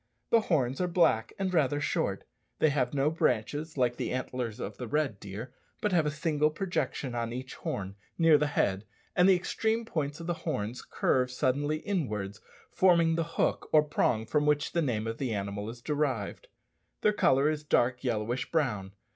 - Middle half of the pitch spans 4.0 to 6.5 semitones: Yes, average, 5.2 semitones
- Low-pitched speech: No, medium, 145 Hz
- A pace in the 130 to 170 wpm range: No, average, 185 wpm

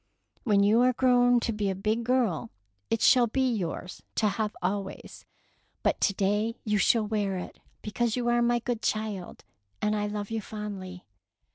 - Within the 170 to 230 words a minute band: Yes, average, 175 wpm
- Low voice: No, high, 215 Hz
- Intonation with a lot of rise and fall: No, average, 2.9 semitones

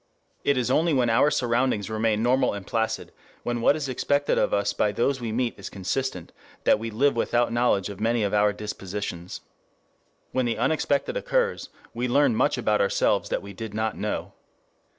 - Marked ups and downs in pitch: No, average, 3.8 semitones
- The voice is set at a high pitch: No, low, 115 Hz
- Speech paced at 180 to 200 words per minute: Yes, average, 190 wpm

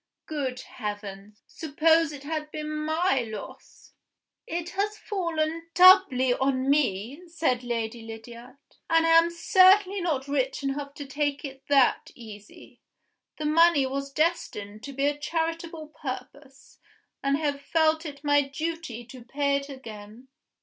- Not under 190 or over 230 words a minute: No, average, 140 wpm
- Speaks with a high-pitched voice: Yes, very high, 285 Hz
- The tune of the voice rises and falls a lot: No, average, 4.2 semitones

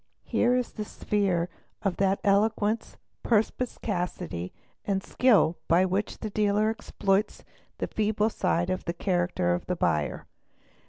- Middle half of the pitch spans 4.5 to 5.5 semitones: No, average, 3.3 semitones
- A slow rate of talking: Yes, slow, 130 wpm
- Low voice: No, high, 200 Hz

